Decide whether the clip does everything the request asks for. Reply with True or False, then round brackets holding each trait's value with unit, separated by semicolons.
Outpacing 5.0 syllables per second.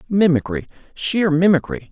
False (4.8 syllables/s)